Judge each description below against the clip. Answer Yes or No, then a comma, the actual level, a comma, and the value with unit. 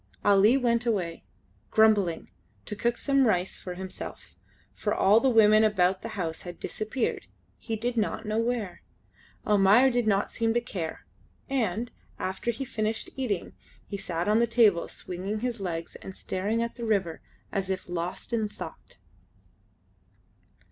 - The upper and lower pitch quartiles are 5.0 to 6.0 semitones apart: No, average, 3.7 semitones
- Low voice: No, high, 215 Hz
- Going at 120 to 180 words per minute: Yes, average, 150 wpm